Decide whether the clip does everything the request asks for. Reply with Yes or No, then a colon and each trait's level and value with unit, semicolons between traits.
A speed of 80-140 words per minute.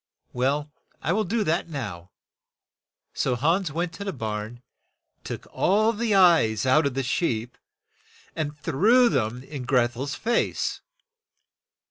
Yes: slow, 135 wpm